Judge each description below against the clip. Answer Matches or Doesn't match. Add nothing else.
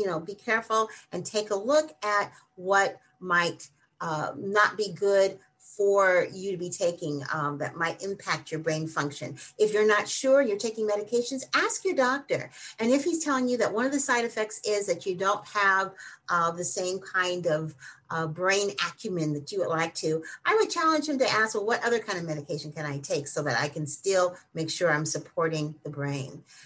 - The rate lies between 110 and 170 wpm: Doesn't match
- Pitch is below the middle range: Doesn't match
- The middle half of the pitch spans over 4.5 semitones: Matches